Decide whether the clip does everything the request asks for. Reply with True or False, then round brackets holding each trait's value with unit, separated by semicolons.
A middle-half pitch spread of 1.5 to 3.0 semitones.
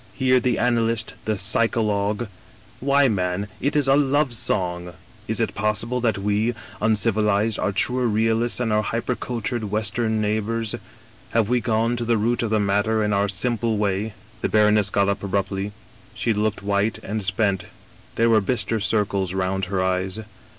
True (2.4 semitones)